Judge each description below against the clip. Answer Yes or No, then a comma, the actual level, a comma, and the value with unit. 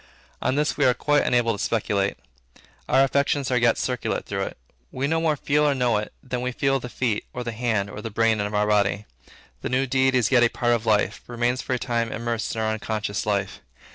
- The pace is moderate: No, fast, 230 wpm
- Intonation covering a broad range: No, average, 3.3 semitones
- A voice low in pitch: Yes, low, 120 Hz